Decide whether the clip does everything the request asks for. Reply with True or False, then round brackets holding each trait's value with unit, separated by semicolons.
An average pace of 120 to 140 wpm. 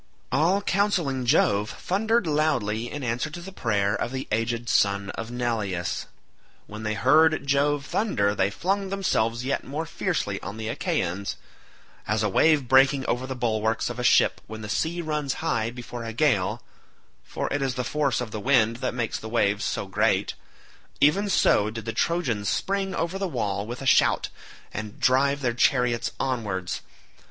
False (170 wpm)